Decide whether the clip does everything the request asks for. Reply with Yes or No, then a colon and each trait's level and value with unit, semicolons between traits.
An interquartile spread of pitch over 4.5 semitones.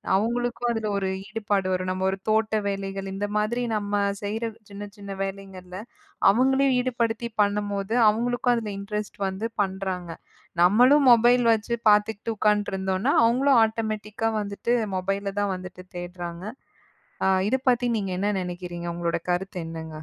No: average, 3.1 semitones